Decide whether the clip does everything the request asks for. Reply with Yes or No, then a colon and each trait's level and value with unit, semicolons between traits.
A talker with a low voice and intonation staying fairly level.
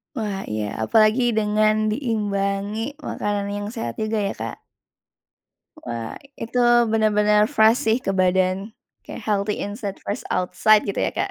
No: high, 210 Hz; narrow, 1.7 semitones